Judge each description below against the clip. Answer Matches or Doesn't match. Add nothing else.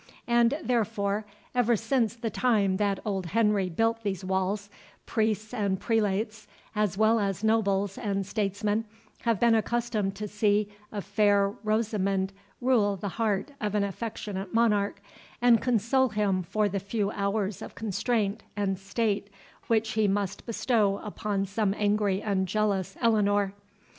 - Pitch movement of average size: Doesn't match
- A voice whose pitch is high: Matches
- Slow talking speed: Doesn't match